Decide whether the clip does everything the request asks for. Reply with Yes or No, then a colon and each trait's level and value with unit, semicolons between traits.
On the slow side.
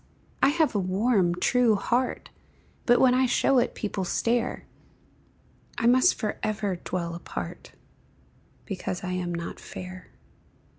Yes: slow, 130 wpm